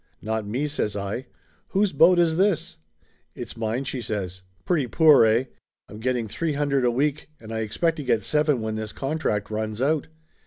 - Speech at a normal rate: Yes, average, 190 wpm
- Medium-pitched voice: No, low, 125 Hz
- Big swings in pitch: Yes, wide, 5.8 semitones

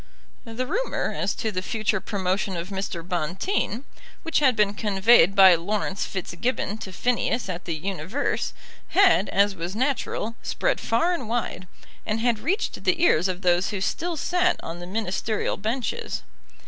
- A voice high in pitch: Yes, high, 210 Hz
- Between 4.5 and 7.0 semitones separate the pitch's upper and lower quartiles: Yes, average, 5.0 semitones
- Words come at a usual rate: Yes, average, 160 wpm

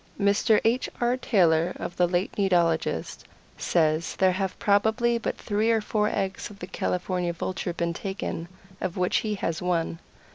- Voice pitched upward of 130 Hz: Yes, medium, 185 Hz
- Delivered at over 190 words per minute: No, average, 160 wpm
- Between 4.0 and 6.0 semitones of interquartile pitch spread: No, average, 3.4 semitones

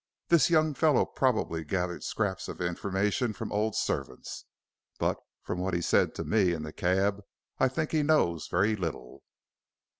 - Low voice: Yes, low, 100 Hz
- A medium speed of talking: Yes, average, 160 wpm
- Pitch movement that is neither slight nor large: No, wide, 6.7 semitones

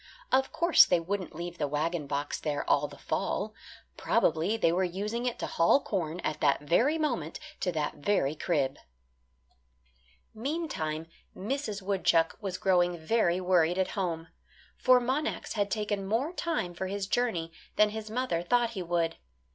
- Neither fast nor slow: Yes, average, 160 wpm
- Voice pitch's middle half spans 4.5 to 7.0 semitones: Yes, wide, 5.4 semitones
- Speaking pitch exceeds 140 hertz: Yes, medium, 185 Hz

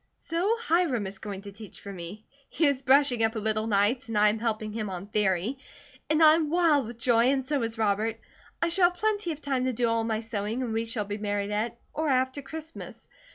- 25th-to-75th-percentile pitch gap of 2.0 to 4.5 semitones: No, average, 5.2 semitones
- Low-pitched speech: No, high, 230 Hz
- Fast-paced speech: Yes, fast, 235 wpm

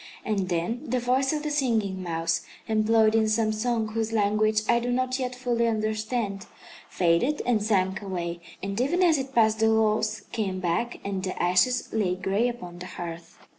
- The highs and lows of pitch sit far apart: No, average, 4.1 semitones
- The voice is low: No, high, 215 Hz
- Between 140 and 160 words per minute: No, average, 180 wpm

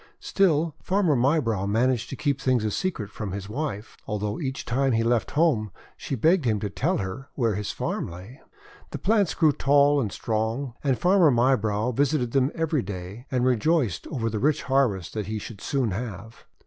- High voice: No, low, 125 Hz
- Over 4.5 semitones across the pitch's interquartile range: Yes, average, 5.1 semitones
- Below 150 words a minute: No, average, 185 wpm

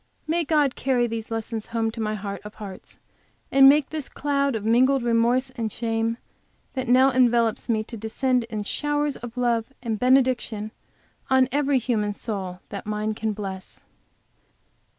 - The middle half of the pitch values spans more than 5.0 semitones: No, average, 3.3 semitones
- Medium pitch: No, high, 235 Hz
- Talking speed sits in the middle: Yes, average, 160 wpm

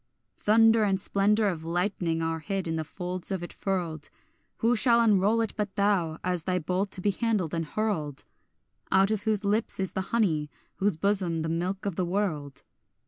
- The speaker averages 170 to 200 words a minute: Yes, average, 190 wpm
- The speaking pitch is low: No, high, 190 Hz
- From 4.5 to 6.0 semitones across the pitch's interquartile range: No, average, 3.8 semitones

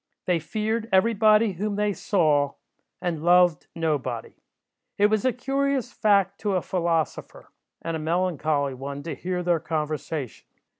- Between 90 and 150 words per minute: Yes, average, 145 wpm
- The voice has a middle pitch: Yes, medium, 180 Hz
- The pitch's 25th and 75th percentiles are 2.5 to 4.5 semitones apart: No, average, 5.1 semitones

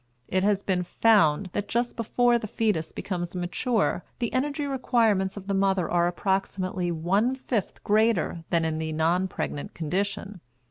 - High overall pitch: Yes, high, 195 Hz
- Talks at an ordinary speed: Yes, average, 155 wpm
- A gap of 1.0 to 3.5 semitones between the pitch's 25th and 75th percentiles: No, average, 4.3 semitones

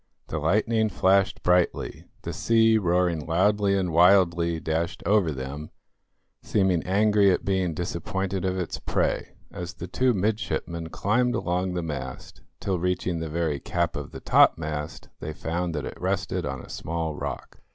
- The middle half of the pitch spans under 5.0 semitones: Yes, average, 3.2 semitones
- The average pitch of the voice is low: Yes, very low, 90 Hz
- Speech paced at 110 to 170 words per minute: Yes, average, 155 wpm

